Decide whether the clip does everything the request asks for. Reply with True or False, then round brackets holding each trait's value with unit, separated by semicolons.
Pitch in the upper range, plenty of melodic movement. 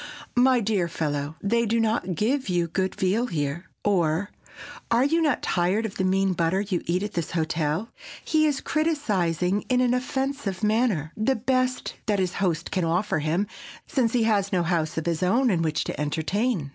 True (195 Hz; 5.8 semitones)